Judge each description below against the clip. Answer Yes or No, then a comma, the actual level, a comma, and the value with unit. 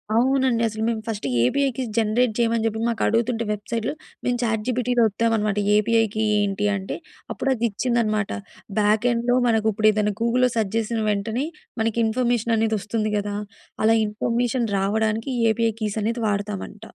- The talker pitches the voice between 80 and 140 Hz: No, high, 225 Hz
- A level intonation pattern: Yes, narrow, 1.9 semitones